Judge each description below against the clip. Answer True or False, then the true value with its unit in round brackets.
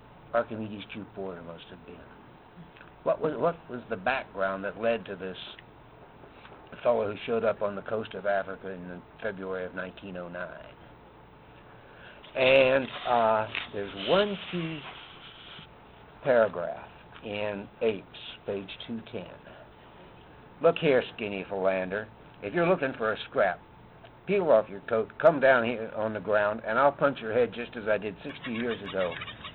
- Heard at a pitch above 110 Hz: False (105 Hz)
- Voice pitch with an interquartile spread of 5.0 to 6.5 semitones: True (5.3 semitones)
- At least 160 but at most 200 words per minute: False (145 wpm)